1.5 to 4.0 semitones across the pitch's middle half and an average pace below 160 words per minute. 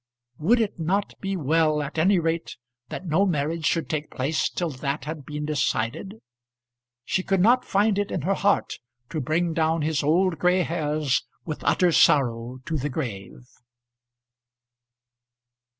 Yes: average, 3.6 semitones; average, 150 wpm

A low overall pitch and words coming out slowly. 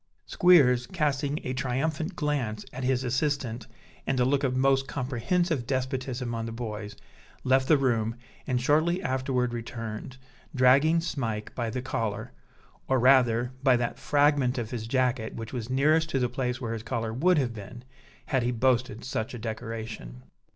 No: low, 125 Hz; average, 165 wpm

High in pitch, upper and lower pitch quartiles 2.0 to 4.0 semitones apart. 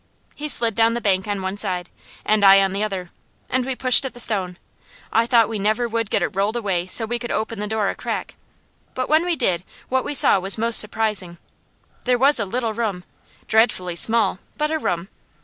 Yes: high, 220 Hz; average, 3.7 semitones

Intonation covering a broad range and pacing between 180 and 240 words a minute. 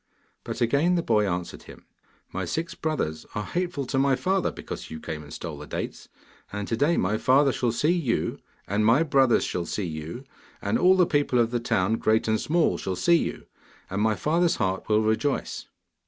Yes: wide, 7.1 semitones; average, 200 wpm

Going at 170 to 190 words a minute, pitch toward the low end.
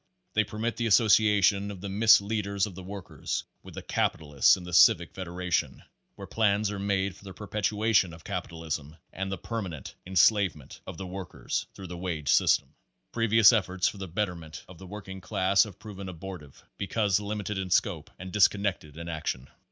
Yes: average, 180 wpm; very low, 95 Hz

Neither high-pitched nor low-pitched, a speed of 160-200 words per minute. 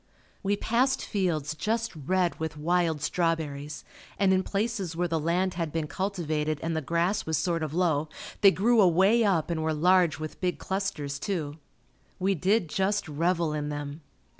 Yes: medium, 170 Hz; average, 170 wpm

